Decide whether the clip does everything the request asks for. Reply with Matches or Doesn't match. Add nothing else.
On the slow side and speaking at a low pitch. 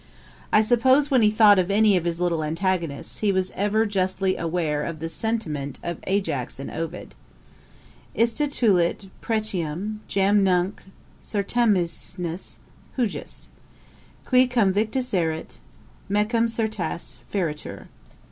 Doesn't match